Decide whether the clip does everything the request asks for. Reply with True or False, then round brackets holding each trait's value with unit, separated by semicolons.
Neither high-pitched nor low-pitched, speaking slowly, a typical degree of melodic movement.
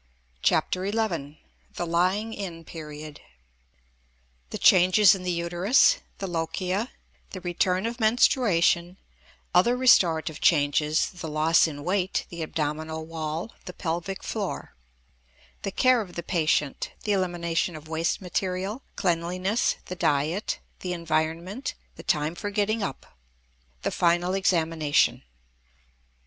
True (175 Hz; 120 wpm; 3.2 semitones)